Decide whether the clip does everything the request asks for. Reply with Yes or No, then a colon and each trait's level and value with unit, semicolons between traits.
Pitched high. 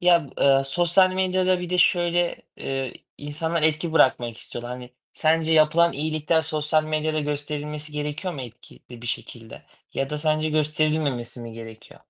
No: medium, 155 Hz